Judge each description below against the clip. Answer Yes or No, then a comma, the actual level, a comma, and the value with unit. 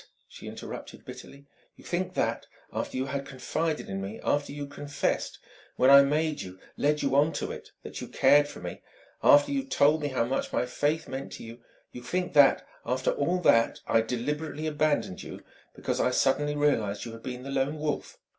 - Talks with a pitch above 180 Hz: No, medium, 140 Hz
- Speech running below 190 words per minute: No, average, 195 wpm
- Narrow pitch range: No, average, 3.1 semitones